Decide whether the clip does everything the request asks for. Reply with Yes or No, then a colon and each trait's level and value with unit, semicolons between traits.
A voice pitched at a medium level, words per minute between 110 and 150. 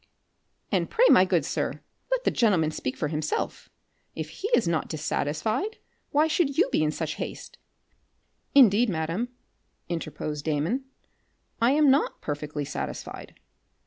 Yes: medium, 175 Hz; average, 140 wpm